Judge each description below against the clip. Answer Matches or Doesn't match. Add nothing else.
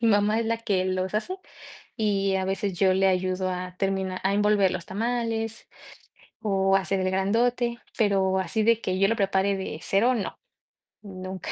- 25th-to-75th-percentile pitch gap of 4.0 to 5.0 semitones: Doesn't match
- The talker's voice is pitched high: Matches